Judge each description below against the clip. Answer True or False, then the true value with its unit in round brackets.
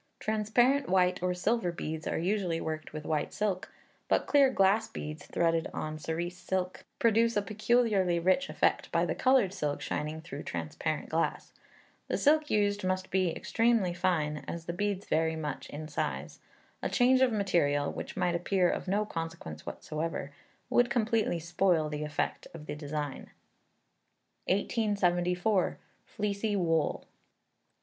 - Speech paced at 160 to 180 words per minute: False (145 wpm)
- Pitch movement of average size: True (4.8 semitones)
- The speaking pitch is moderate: True (180 Hz)